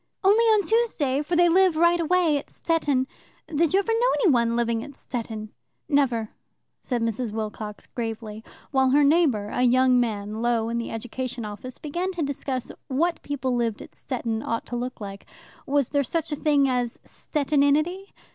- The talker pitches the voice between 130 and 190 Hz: No, very high, 260 Hz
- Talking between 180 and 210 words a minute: Yes, average, 185 wpm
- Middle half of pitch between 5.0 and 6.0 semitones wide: Yes, wide, 5.6 semitones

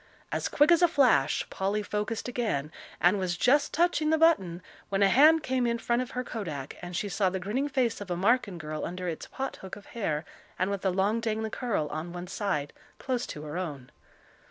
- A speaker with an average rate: No, fast, 215 wpm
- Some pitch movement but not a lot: No, wide, 5.9 semitones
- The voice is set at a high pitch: Yes, high, 205 Hz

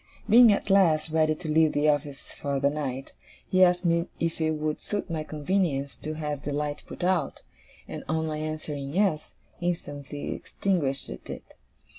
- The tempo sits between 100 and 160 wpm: No, average, 170 wpm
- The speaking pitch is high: No, medium, 155 Hz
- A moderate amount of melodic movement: Yes, average, 3.1 semitones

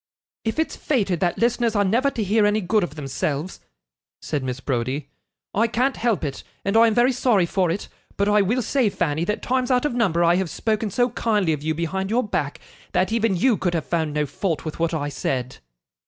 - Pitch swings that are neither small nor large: No, wide, 6.2 semitones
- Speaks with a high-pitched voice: Yes, high, 195 Hz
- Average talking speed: No, fast, 220 wpm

